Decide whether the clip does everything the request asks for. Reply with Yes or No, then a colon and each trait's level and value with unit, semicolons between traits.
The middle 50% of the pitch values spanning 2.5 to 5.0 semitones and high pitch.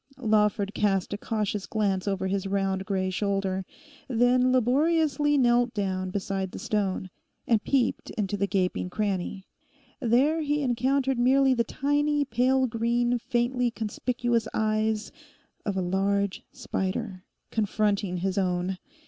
Yes: average, 4.3 semitones; high, 215 Hz